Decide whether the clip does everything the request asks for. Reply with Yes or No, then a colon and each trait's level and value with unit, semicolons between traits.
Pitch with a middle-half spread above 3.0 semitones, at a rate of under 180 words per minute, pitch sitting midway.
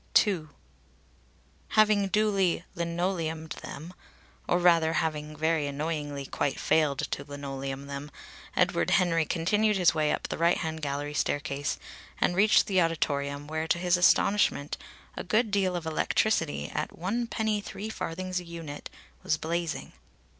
Yes: average, 3.8 semitones; average, 140 wpm; medium, 165 Hz